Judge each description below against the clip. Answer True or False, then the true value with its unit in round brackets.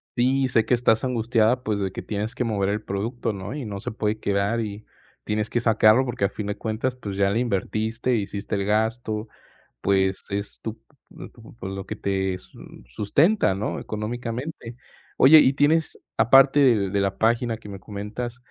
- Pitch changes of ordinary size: True (3.2 semitones)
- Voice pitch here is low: True (110 Hz)